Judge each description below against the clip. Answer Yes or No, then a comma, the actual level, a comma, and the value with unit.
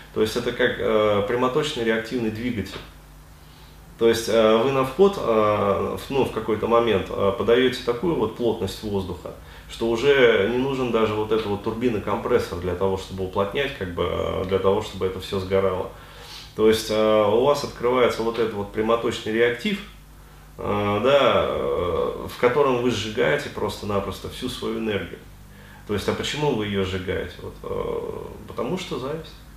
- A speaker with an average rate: No, fast, 165 wpm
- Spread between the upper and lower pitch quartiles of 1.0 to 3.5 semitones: No, average, 4.1 semitones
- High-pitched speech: No, low, 110 Hz